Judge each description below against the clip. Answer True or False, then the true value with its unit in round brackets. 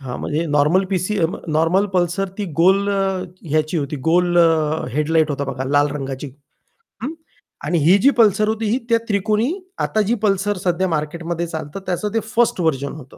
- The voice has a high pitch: False (175 Hz)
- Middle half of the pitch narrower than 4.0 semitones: False (4.6 semitones)